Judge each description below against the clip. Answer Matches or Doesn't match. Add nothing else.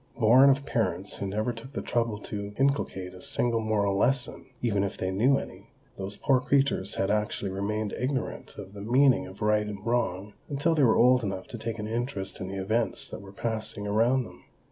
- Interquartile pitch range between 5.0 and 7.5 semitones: Doesn't match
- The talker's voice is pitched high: Doesn't match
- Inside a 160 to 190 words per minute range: Doesn't match